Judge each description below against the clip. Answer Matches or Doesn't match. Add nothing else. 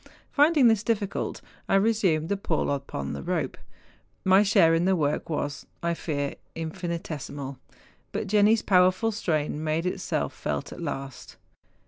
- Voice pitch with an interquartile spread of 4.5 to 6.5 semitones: Matches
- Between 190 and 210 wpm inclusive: Doesn't match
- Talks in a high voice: Doesn't match